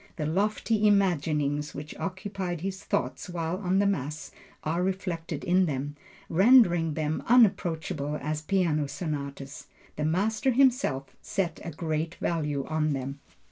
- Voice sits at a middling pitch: Yes, medium, 165 Hz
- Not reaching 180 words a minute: Yes, slow, 135 wpm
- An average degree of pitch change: Yes, average, 4.2 semitones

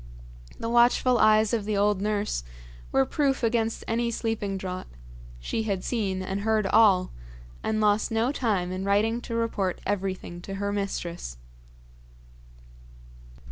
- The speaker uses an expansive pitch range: No, average, 2.9 semitones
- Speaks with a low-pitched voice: No, high, 210 Hz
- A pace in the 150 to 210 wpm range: No, average, 140 wpm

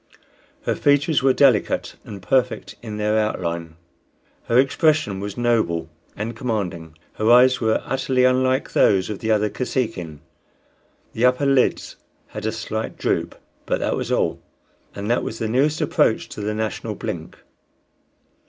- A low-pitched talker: Yes, low, 110 Hz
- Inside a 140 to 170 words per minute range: Yes, average, 150 wpm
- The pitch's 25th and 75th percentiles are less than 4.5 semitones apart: Yes, average, 3.7 semitones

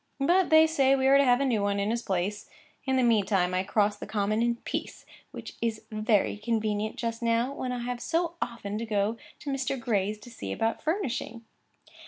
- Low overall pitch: No, high, 230 Hz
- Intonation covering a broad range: No, average, 4.0 semitones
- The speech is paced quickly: Yes, fast, 210 wpm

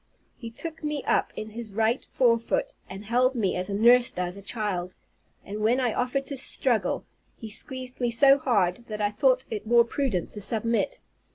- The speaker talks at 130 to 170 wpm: No, average, 190 wpm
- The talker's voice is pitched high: Yes, high, 235 Hz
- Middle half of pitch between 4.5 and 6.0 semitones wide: No, average, 3.5 semitones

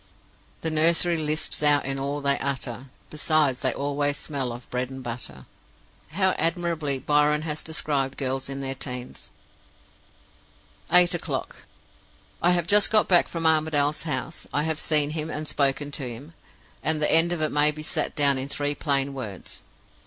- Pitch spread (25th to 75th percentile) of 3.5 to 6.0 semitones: No, narrow, 2.6 semitones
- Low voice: No, medium, 145 Hz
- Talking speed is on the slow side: No, average, 165 wpm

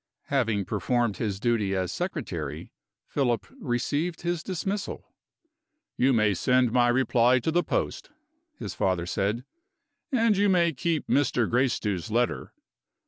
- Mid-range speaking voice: No, low, 125 Hz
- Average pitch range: No, wide, 6.9 semitones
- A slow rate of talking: Yes, slow, 130 wpm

